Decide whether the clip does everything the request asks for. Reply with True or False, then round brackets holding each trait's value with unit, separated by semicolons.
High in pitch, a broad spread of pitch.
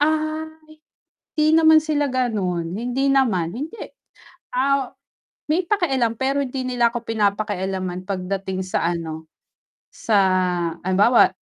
True (235 Hz; 6.6 semitones)